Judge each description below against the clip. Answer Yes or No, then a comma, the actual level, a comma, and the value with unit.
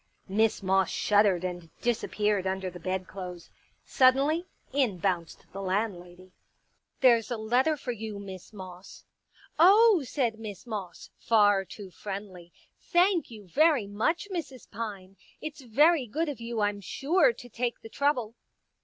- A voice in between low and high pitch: No, high, 215 Hz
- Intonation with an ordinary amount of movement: No, wide, 5.7 semitones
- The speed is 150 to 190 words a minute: Yes, average, 155 wpm